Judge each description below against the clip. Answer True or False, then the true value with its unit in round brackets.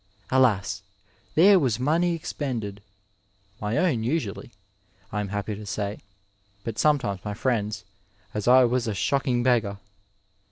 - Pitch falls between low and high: False (115 Hz)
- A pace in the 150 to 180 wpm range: False (135 wpm)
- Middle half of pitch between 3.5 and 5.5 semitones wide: True (4.2 semitones)